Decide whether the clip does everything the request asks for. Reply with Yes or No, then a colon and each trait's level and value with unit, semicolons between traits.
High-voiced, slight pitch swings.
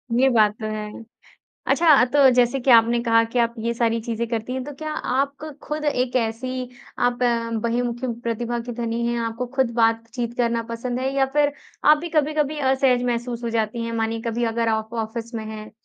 Yes: high, 240 Hz; narrow, 2.2 semitones